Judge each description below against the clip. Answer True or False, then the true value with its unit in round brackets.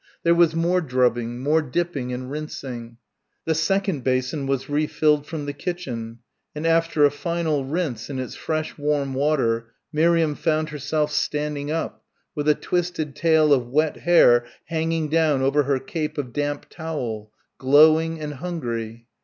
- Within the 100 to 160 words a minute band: True (155 wpm)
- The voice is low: False (150 Hz)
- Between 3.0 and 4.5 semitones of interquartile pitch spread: True (3.6 semitones)